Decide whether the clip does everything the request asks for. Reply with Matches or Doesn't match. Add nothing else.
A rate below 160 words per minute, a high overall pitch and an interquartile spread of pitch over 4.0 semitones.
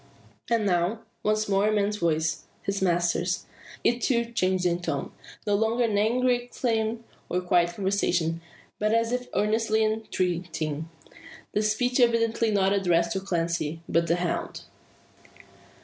Matches